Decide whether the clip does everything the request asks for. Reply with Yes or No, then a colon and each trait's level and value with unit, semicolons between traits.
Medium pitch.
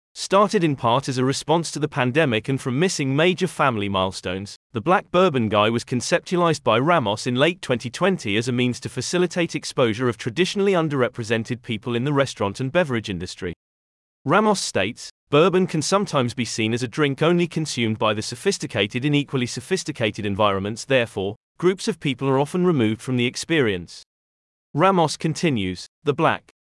No: low, 130 Hz